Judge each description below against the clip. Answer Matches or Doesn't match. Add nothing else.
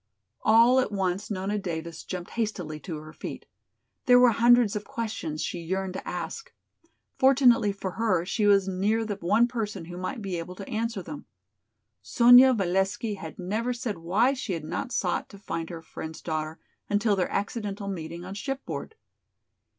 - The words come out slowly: Doesn't match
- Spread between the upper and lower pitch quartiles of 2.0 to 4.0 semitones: Doesn't match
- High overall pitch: Matches